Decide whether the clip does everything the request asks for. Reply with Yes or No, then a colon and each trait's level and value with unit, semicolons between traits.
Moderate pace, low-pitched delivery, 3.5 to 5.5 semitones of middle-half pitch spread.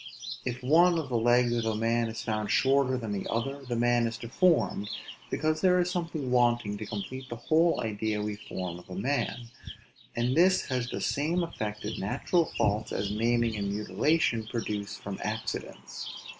Yes: average, 180 wpm; low, 120 Hz; average, 4.5 semitones